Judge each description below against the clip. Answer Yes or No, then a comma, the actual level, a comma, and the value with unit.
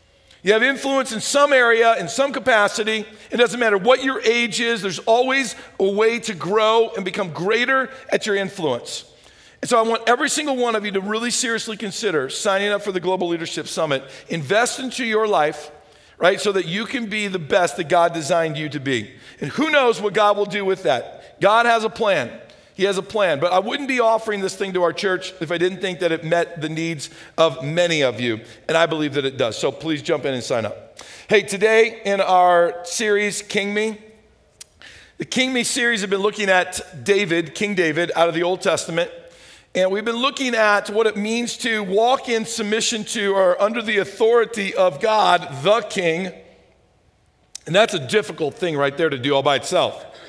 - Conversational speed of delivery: No, fast, 210 wpm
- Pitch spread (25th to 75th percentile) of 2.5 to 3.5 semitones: No, average, 4.6 semitones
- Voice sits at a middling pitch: No, high, 205 Hz